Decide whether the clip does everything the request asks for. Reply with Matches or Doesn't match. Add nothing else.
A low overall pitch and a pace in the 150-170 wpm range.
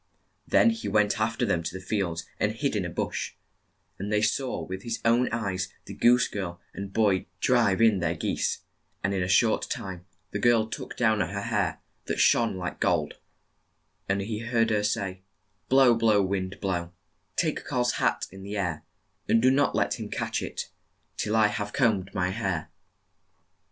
Doesn't match